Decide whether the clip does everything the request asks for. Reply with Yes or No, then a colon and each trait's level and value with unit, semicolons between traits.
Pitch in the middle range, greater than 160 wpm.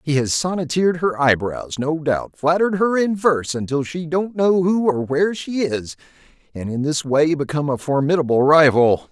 Yes: medium, 155 Hz; average, 180 wpm